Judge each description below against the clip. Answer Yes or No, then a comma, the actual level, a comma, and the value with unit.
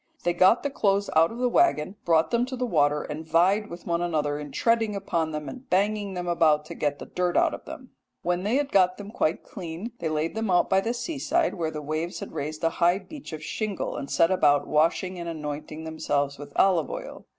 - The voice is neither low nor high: Yes, medium, 175 Hz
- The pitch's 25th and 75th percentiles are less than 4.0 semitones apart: No, average, 4.9 semitones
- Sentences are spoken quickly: Yes, fast, 230 wpm